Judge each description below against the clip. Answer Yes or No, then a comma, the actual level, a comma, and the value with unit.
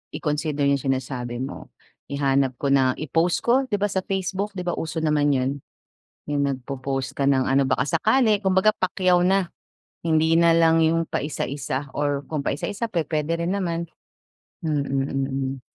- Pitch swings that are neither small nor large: Yes, average, 4.3 semitones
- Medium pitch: Yes, medium, 150 Hz